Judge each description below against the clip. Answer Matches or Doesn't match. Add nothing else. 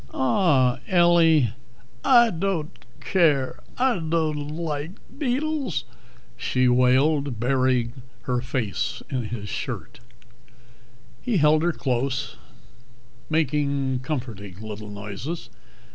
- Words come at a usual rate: Doesn't match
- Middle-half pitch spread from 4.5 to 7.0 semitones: Matches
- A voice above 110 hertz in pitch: Matches